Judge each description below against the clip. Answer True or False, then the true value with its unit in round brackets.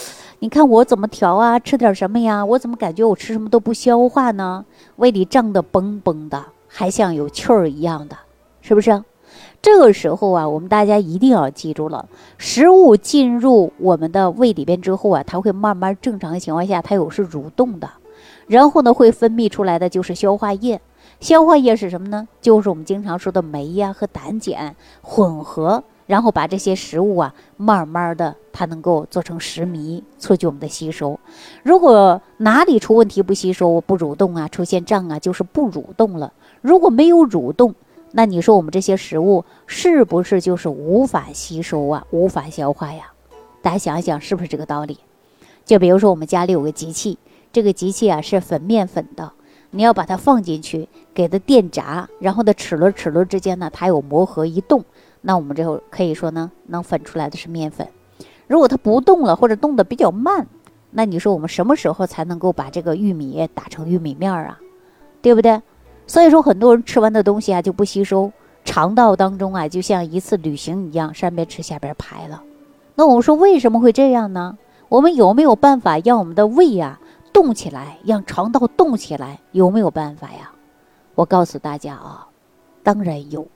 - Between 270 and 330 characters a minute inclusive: True (290 characters per minute)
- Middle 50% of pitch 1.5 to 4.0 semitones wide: False (5.4 semitones)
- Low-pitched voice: False (195 Hz)